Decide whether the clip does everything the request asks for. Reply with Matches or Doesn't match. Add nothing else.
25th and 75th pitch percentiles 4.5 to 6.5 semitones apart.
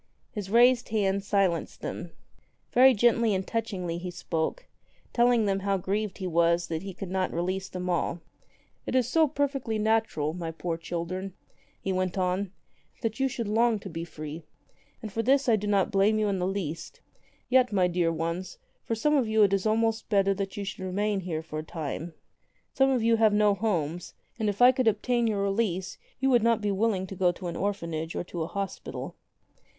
Doesn't match